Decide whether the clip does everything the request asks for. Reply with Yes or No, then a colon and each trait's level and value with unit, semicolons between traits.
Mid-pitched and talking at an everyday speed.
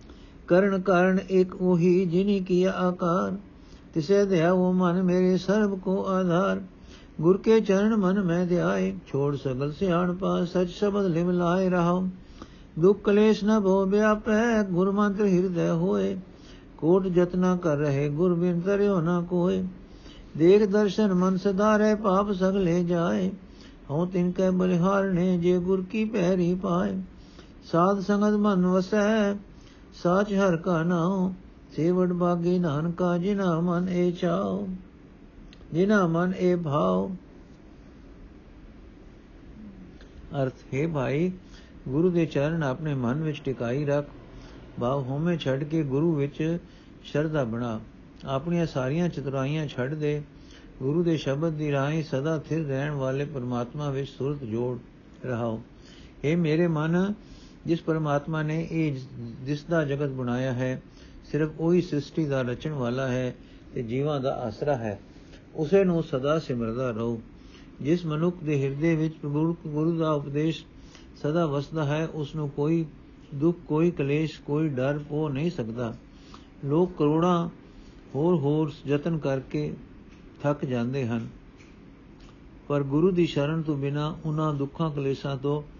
Yes: medium, 165 Hz; average, 135 wpm